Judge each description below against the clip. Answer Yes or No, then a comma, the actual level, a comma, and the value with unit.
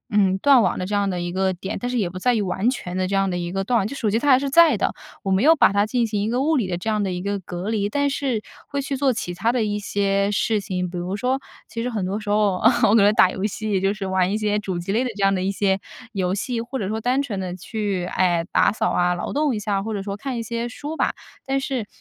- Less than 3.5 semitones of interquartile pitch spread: No, average, 3.9 semitones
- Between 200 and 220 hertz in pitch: Yes, high, 205 Hz